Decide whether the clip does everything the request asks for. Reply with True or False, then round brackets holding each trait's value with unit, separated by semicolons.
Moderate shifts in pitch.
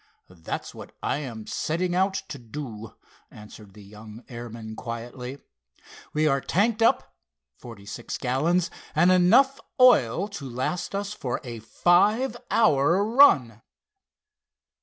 False (8.4 semitones)